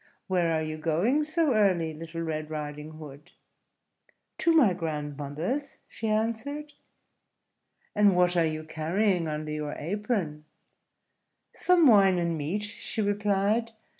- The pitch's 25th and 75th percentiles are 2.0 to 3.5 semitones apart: No, wide, 5.6 semitones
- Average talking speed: No, slow, 125 wpm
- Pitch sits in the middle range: Yes, medium, 175 Hz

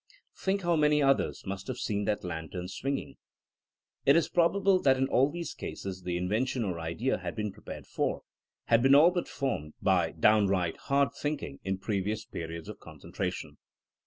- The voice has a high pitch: No, low, 115 Hz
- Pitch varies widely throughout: Yes, wide, 7.2 semitones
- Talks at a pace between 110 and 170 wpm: No, average, 180 wpm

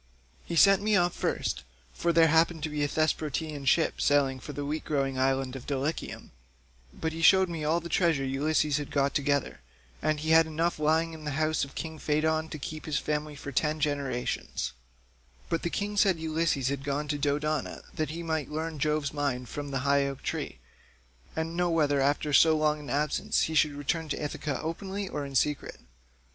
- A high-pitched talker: No, medium, 150 Hz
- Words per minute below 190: No, average, 200 wpm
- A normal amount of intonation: No, narrow, 2.2 semitones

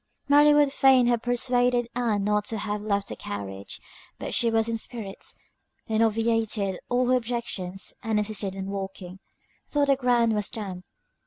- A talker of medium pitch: No, high, 225 Hz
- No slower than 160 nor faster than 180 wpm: Yes, average, 165 wpm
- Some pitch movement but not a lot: Yes, average, 3.5 semitones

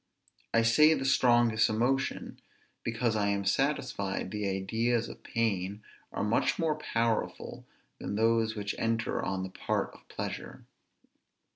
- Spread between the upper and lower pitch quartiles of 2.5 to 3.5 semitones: Yes, average, 2.8 semitones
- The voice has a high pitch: No, low, 115 Hz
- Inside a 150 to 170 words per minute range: No, slow, 135 wpm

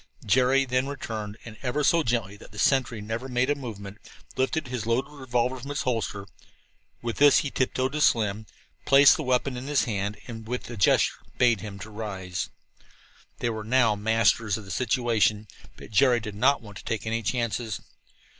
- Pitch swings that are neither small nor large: Yes, average, 3.3 semitones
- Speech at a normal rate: Yes, average, 180 wpm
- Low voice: Yes, low, 115 Hz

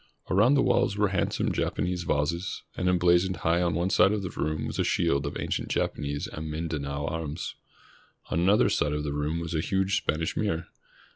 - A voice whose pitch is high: No, very low, 85 Hz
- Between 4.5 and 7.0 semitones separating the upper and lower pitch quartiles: No, average, 3.4 semitones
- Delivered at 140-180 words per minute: No, average, 195 wpm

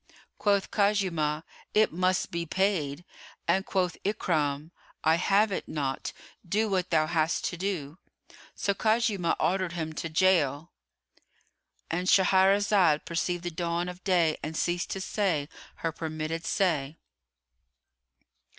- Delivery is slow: Yes, slow, 125 wpm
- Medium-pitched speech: Yes, medium, 175 Hz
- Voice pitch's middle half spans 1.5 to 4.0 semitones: Yes, average, 3.4 semitones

